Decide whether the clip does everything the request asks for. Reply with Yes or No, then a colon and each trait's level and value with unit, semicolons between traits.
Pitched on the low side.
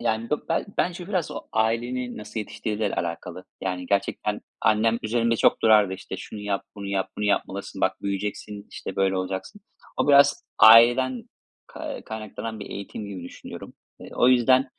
Yes: low, 110 Hz